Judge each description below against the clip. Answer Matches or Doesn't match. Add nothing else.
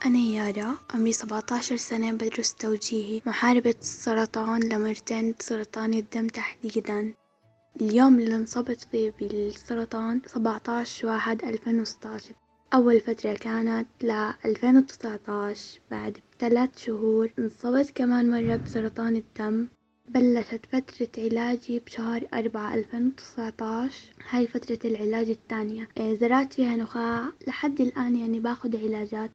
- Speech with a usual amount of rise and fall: Doesn't match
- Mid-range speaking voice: Doesn't match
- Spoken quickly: Doesn't match